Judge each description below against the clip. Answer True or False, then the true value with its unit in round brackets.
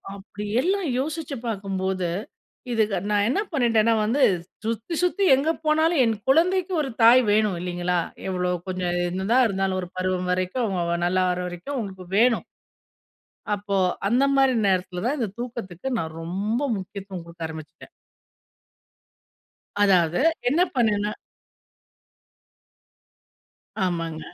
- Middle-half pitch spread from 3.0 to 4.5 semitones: False (5.5 semitones)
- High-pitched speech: True (200 Hz)